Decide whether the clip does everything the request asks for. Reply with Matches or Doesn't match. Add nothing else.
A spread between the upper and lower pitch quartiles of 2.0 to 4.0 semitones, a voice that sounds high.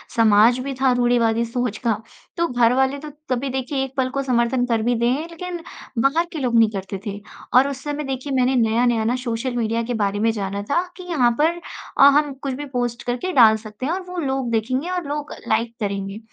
Matches